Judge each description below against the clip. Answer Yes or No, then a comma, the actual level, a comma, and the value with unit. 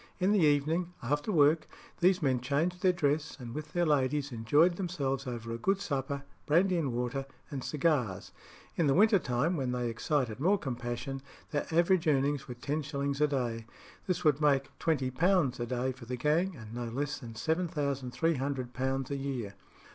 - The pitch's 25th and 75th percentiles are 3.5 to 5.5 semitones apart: Yes, average, 4.3 semitones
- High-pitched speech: No, medium, 140 Hz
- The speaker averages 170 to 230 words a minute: Yes, average, 175 wpm